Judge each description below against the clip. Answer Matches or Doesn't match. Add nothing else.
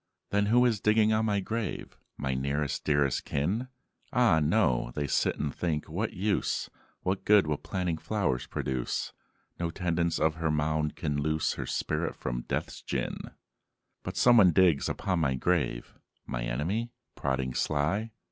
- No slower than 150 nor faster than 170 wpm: Matches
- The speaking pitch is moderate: Doesn't match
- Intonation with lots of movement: Matches